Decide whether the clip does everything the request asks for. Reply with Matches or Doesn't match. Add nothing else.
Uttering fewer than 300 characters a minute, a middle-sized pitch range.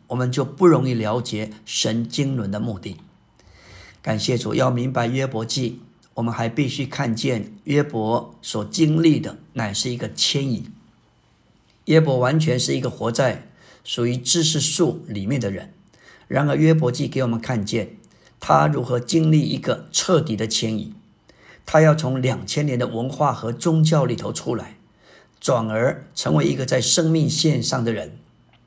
Matches